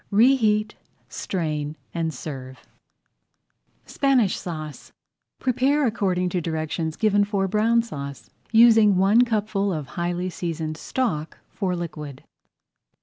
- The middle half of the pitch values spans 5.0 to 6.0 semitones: Yes, wide, 5.6 semitones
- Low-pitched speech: No, medium, 185 Hz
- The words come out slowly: Yes, slow, 105 wpm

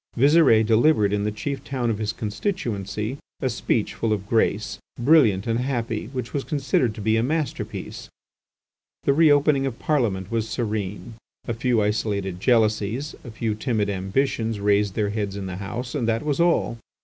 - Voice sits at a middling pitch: No, low, 115 Hz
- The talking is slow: No, average, 175 wpm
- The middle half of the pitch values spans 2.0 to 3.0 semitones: No, average, 4.1 semitones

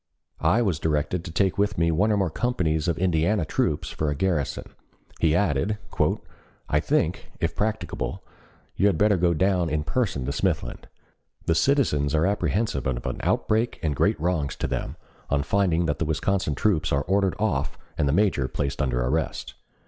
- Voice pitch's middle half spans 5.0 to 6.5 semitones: Yes, average, 5.3 semitones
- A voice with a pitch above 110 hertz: No, very low, 85 Hz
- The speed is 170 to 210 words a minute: Yes, average, 180 wpm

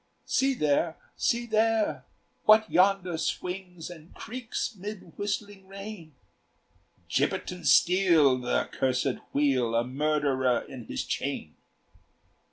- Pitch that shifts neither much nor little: No, wide, 6.6 semitones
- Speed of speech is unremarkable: No, slow, 110 wpm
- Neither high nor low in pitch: Yes, medium, 175 Hz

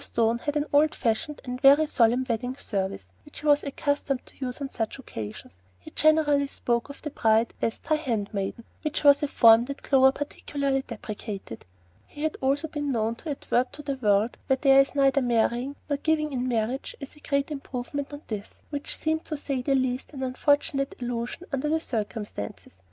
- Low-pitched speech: No, very high, 270 Hz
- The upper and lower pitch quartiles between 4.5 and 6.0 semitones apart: No, average, 3.6 semitones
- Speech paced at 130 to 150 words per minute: No, average, 190 wpm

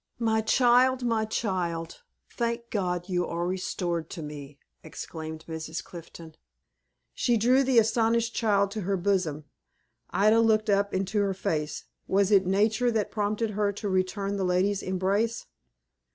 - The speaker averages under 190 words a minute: Yes, average, 145 wpm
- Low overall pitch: No, high, 200 Hz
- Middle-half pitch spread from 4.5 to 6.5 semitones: No, average, 3.8 semitones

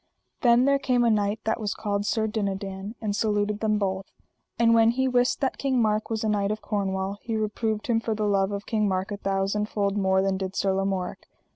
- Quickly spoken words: Yes, fast, 225 wpm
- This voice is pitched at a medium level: No, high, 210 Hz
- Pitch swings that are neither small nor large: No, narrow, 2.2 semitones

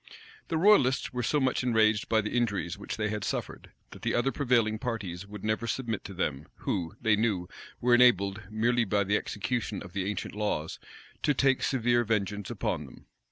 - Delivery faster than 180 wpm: Yes, average, 190 wpm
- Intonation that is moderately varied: Yes, average, 3.4 semitones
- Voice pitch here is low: Yes, low, 110 Hz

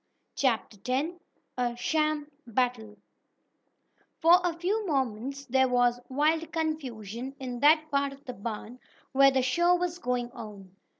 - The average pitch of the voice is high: Yes, very high, 265 Hz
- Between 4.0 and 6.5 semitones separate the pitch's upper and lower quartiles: Yes, average, 4.3 semitones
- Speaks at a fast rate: No, slow, 135 wpm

